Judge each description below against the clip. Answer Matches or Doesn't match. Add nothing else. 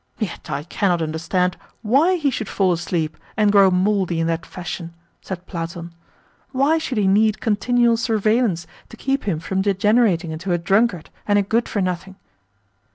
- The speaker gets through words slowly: Doesn't match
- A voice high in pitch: Matches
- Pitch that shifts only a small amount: Doesn't match